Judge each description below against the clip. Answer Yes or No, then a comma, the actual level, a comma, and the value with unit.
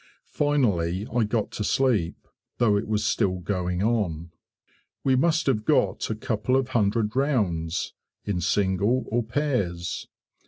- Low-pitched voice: Yes, low, 105 Hz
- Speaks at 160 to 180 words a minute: No, slow, 135 wpm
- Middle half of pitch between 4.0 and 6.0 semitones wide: Yes, wide, 5.6 semitones